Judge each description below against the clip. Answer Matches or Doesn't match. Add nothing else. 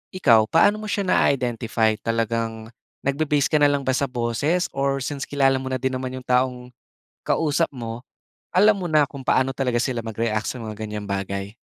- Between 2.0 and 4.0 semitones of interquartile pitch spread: Matches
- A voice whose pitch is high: Doesn't match